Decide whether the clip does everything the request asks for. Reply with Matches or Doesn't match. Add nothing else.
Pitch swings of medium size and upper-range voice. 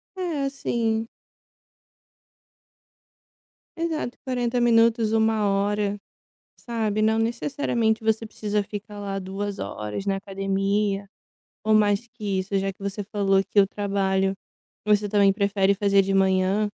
Doesn't match